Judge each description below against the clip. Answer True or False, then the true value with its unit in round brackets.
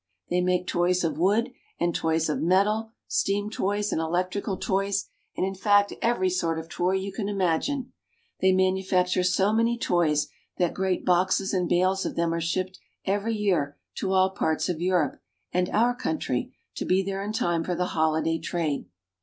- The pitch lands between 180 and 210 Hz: True (185 Hz)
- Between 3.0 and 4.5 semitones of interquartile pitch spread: False (2.4 semitones)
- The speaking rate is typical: True (180 wpm)